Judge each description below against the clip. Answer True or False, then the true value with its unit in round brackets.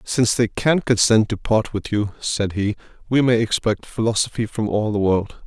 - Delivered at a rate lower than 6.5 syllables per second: True (4.9 syllables/s)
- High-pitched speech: False (110 Hz)